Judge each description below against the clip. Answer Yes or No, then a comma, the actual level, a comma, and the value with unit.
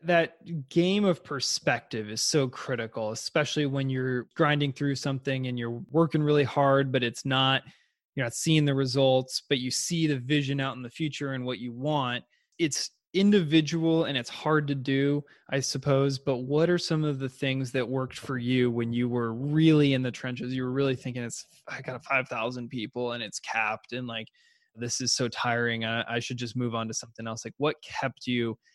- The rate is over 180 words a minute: Yes, average, 200 wpm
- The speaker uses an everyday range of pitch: Yes, average, 3.1 semitones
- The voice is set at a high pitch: No, low, 135 Hz